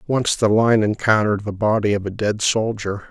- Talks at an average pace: Yes, average, 195 wpm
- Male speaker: Yes, male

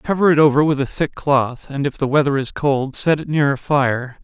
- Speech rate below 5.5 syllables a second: Yes, 5.0 syllables/s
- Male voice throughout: Yes, male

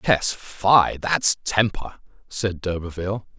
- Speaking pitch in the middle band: No, very low, 95 Hz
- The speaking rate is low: Yes, slow, 90 wpm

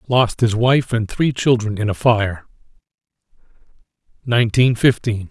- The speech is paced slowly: Yes, slow, 125 wpm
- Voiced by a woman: No, male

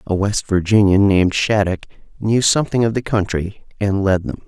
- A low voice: Yes, low, 100 Hz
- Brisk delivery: No, average, 175 wpm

